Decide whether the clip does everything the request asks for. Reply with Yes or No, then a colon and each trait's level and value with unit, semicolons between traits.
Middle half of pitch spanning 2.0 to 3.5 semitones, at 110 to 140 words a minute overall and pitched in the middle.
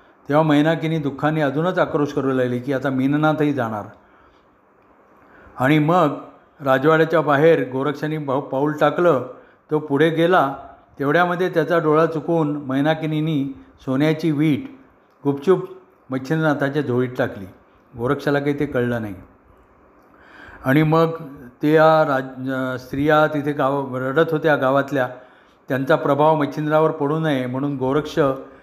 Yes: average, 2.9 semitones; average, 115 wpm; medium, 150 Hz